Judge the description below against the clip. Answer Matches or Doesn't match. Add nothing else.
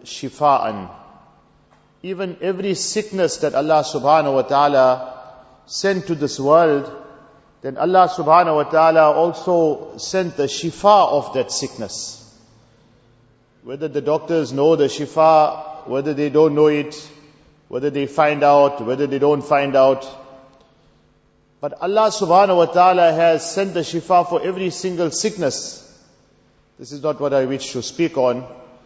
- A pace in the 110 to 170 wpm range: Matches